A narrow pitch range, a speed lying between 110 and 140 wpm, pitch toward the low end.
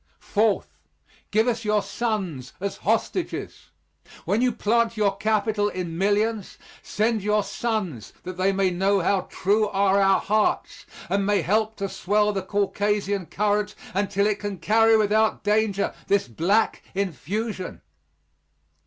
No: narrow, 1.9 semitones; slow, 135 wpm; high, 205 Hz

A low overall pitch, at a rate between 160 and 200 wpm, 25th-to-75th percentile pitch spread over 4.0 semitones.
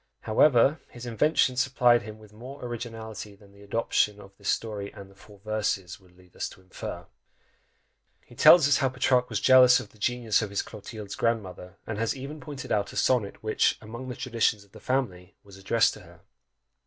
No: low, 110 Hz; average, 195 wpm; average, 3.7 semitones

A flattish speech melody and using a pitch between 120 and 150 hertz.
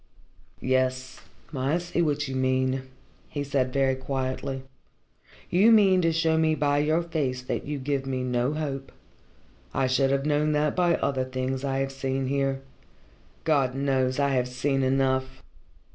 Yes: narrow, 2.2 semitones; low, 135 Hz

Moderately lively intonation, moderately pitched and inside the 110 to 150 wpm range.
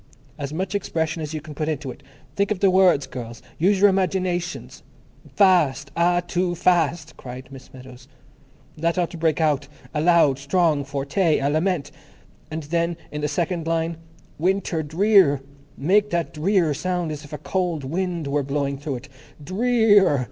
No: average, 4.1 semitones; medium, 160 Hz; average, 165 wpm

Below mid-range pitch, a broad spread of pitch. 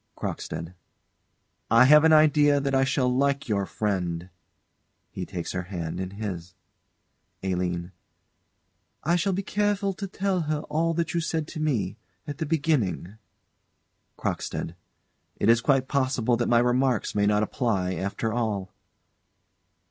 Yes: low, 125 Hz; wide, 8.0 semitones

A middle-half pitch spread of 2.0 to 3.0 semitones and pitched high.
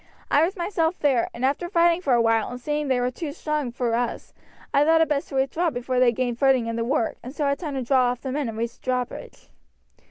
No: average, 3.6 semitones; very high, 265 Hz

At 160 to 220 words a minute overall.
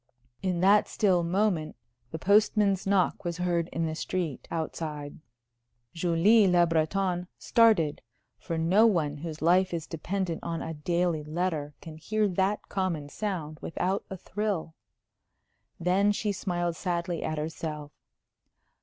No: slow, 135 wpm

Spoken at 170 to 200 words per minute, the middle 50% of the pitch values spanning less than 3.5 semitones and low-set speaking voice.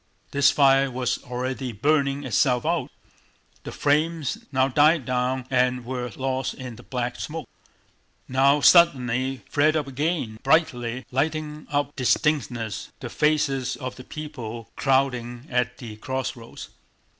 No: slow, 135 wpm; average, 2.8 semitones; low, 130 Hz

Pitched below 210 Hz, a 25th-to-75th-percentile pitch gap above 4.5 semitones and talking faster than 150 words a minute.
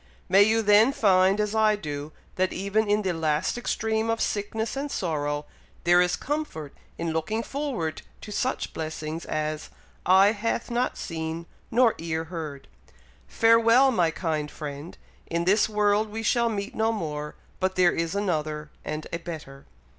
Yes: medium, 185 Hz; wide, 5.5 semitones; average, 160 wpm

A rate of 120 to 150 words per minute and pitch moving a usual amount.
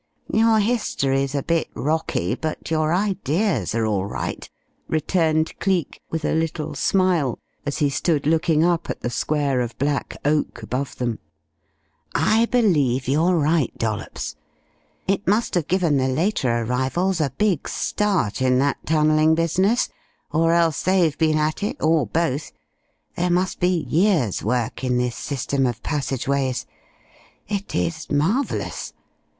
Yes: average, 145 wpm; average, 4.8 semitones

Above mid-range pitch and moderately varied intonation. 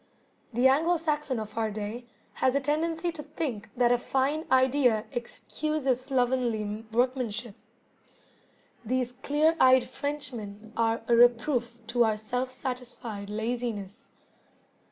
Yes: high, 245 Hz; average, 3.3 semitones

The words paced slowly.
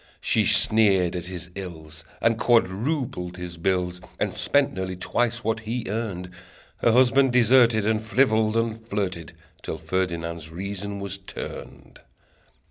Yes: slow, 130 wpm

